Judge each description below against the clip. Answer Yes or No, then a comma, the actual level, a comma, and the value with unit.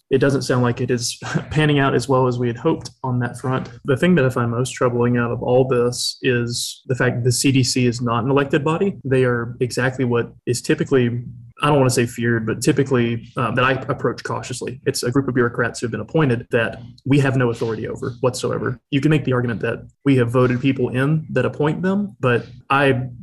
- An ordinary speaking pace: No, fast, 235 wpm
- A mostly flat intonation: Yes, narrow, 2.2 semitones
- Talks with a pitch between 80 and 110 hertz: No, low, 125 Hz